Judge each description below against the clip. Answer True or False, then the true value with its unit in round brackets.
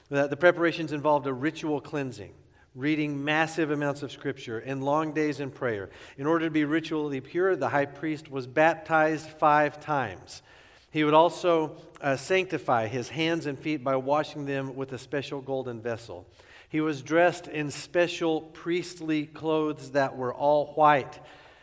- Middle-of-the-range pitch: True (150 Hz)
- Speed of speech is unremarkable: True (160 wpm)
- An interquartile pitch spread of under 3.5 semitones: True (2.4 semitones)